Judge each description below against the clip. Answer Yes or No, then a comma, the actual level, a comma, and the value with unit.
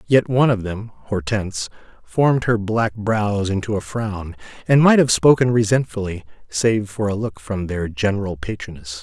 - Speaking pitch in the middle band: No, low, 105 Hz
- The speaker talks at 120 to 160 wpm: Yes, average, 155 wpm